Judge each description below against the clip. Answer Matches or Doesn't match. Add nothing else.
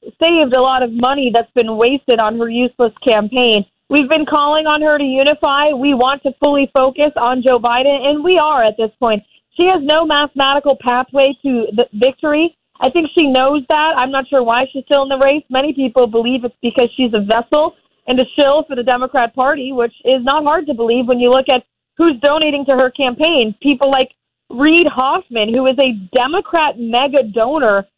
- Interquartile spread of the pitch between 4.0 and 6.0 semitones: Doesn't match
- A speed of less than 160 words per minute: Doesn't match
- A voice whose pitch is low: Doesn't match